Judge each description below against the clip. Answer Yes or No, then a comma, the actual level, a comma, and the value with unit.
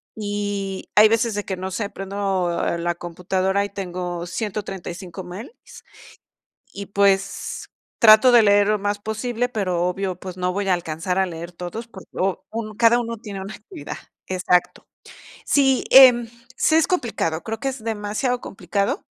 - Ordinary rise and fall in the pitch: Yes, average, 3.4 semitones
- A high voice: Yes, high, 200 Hz